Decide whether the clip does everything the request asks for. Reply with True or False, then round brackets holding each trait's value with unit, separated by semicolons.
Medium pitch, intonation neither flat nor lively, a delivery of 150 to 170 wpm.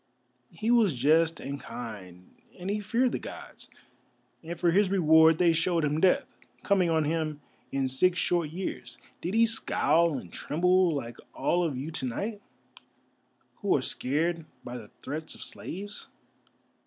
True (165 Hz; 4.3 semitones; 155 wpm)